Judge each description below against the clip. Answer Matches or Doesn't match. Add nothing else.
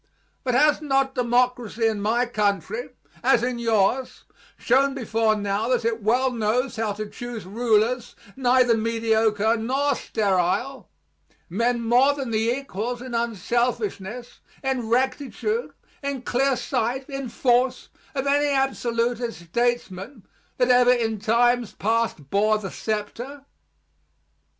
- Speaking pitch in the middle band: Doesn't match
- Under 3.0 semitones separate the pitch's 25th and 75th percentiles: Matches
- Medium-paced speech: Doesn't match